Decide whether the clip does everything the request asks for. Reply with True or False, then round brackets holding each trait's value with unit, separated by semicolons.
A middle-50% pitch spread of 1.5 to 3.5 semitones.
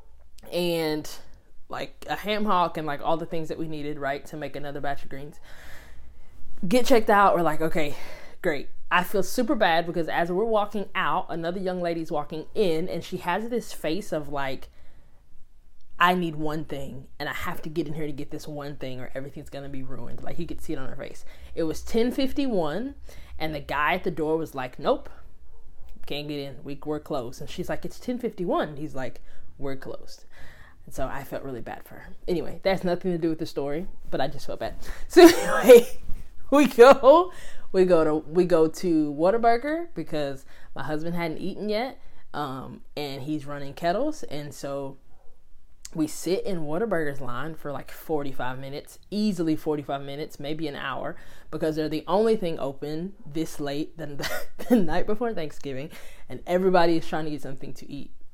False (4.2 semitones)